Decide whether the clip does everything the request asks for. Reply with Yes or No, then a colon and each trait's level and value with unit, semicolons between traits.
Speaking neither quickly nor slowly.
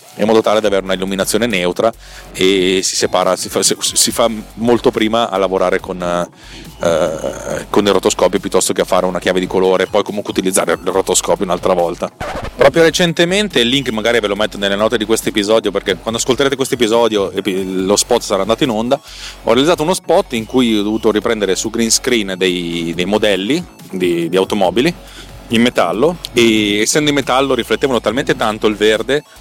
No: fast, 190 wpm